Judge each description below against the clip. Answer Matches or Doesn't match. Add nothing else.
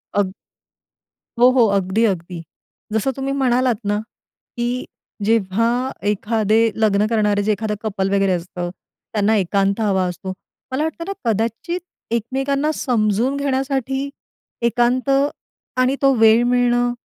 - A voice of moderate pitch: Doesn't match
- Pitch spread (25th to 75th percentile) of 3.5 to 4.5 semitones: Matches